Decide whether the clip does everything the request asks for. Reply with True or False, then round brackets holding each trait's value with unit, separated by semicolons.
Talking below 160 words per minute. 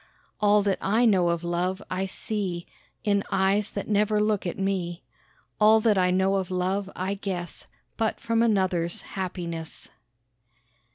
True (150 wpm)